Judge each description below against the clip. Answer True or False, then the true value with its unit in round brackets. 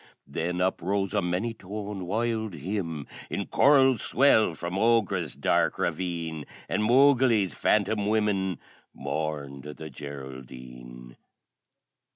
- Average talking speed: False (105 wpm)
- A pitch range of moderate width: False (5.8 semitones)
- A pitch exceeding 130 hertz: False (95 Hz)